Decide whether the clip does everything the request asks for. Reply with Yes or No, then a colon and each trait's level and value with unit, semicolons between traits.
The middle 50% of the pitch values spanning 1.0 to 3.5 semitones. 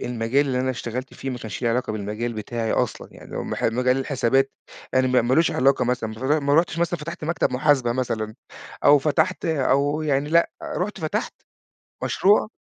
No: average, 3.9 semitones